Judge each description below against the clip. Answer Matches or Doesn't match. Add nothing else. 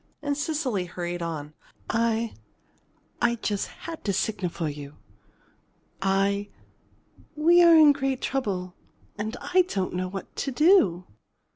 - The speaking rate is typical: Doesn't match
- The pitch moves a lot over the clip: Matches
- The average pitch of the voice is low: Doesn't match